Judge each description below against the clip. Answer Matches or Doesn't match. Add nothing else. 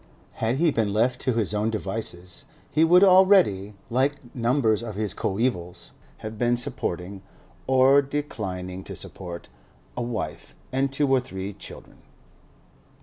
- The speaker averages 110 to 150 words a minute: Matches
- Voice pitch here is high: Doesn't match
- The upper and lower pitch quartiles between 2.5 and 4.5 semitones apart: Doesn't match